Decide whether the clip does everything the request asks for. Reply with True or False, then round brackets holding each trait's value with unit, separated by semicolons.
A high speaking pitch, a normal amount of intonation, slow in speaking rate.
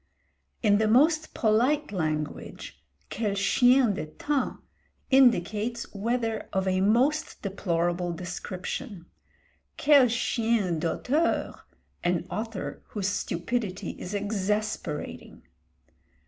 True (210 Hz; 4.7 semitones; 90 wpm)